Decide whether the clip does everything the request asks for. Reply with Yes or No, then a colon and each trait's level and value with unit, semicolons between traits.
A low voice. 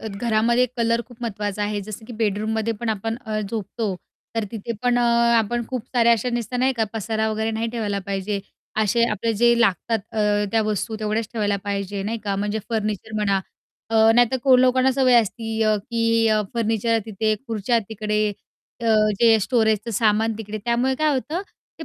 No: high, 220 Hz